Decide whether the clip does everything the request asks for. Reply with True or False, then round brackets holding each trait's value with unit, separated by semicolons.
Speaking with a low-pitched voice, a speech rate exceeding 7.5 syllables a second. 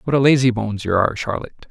True (120 Hz; 7.8 syllables/s)